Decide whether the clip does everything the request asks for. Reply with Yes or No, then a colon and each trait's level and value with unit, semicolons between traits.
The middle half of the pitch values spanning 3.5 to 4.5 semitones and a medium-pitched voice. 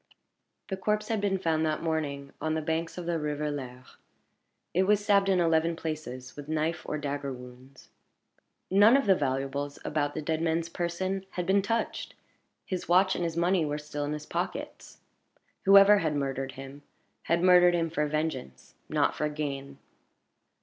Yes: average, 3.9 semitones; medium, 160 Hz